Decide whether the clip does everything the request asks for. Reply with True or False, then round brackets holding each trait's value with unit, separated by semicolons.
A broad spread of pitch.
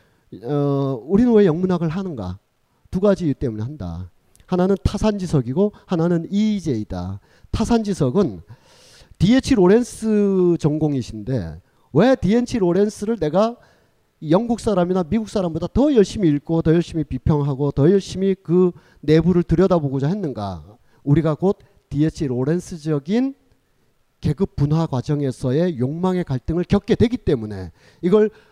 True (6.1 semitones)